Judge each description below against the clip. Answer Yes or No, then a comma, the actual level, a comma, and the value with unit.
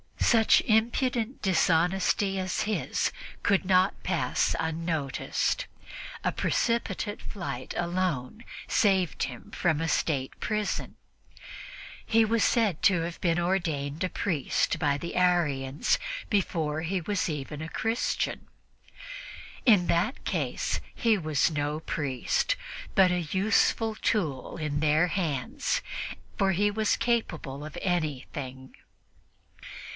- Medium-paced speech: No, slow, 115 wpm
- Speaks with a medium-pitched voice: Yes, medium, 175 Hz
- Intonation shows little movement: No, average, 5.3 semitones